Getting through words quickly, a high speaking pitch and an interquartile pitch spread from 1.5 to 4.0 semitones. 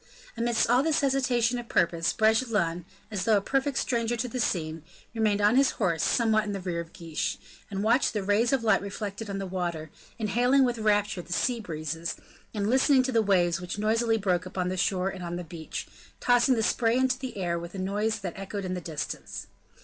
No: fast, 210 wpm; high, 205 Hz; average, 4.7 semitones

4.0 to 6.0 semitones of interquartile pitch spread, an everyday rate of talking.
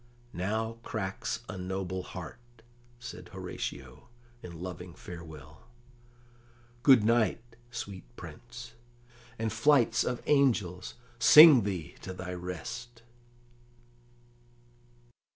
No: average, 4.6 semitones; slow, 90 wpm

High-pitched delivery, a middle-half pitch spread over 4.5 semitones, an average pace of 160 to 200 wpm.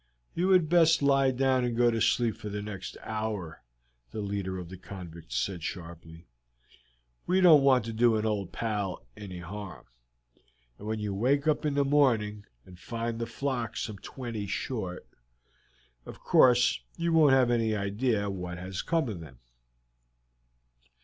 No: low, 110 Hz; average, 5.3 semitones; average, 165 wpm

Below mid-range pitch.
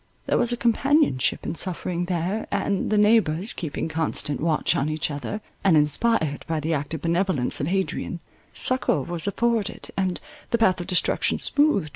No: medium, 175 Hz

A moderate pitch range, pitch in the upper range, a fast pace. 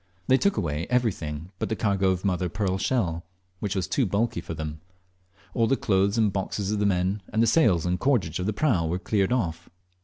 No: average, 3.9 semitones; very low, 95 Hz; fast, 220 wpm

